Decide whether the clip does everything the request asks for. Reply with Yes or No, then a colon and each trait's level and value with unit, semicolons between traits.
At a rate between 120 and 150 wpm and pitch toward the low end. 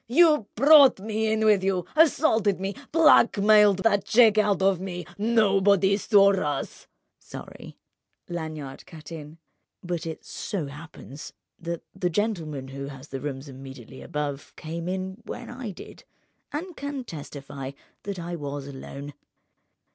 No: average, 140 wpm; high, 190 Hz